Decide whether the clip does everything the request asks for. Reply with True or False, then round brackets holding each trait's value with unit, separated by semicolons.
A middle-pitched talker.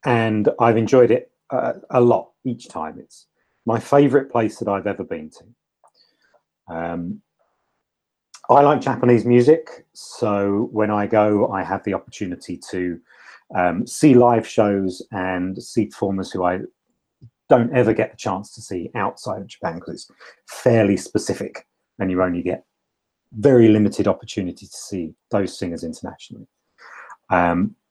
False (105 Hz)